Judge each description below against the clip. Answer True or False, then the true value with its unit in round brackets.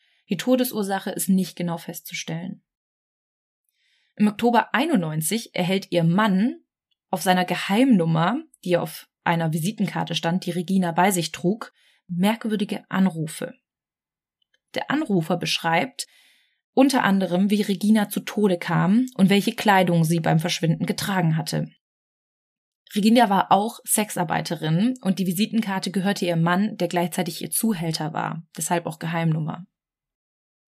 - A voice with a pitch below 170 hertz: False (190 Hz)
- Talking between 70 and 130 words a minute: True (125 wpm)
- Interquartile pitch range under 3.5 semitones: False (3.8 semitones)